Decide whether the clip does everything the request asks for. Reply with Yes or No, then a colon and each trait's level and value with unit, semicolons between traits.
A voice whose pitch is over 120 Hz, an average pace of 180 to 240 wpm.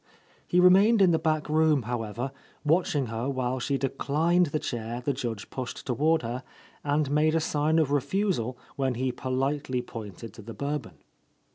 No: medium, 140 Hz; average, 170 wpm